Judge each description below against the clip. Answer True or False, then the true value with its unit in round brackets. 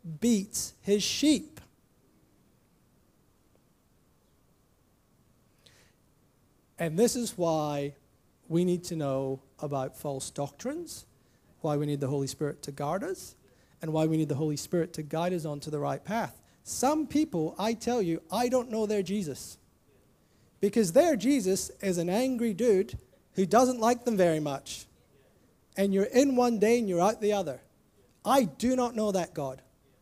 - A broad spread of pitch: True (7.9 semitones)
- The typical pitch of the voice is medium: True (180 Hz)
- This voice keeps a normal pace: True (150 wpm)